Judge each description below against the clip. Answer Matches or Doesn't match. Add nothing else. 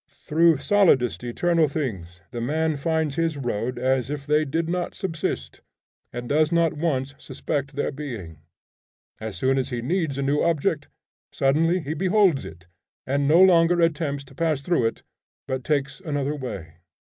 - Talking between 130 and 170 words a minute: Matches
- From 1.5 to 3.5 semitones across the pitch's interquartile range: Doesn't match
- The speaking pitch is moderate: Matches